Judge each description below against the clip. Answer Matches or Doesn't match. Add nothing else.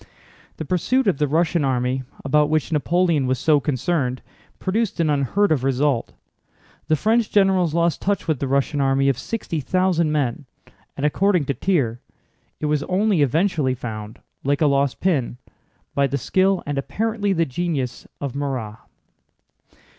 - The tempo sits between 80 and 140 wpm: Doesn't match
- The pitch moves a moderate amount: Matches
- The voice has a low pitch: Doesn't match